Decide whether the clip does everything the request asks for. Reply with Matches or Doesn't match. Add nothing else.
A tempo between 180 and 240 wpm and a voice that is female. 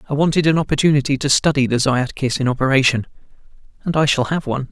Doesn't match